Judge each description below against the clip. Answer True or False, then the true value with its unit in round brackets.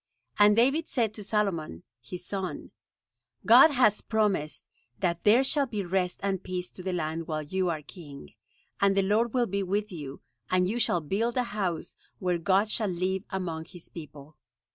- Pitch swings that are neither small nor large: True (3.7 semitones)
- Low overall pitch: False (190 Hz)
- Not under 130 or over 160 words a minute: False (180 wpm)